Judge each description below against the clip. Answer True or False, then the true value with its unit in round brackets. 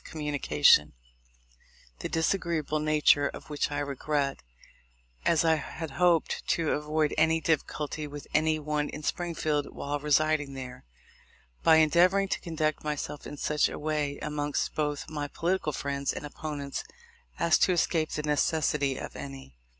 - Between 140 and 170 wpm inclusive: True (145 wpm)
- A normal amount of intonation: False (1.6 semitones)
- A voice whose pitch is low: False (150 Hz)